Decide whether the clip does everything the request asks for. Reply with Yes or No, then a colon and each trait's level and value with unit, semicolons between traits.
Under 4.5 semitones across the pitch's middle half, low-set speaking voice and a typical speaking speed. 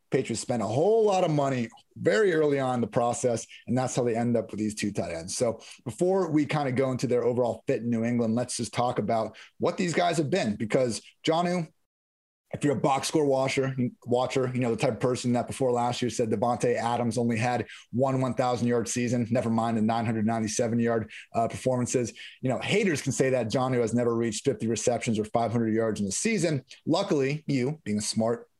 No: average, 2.7 semitones; low, 120 Hz; fast, 220 wpm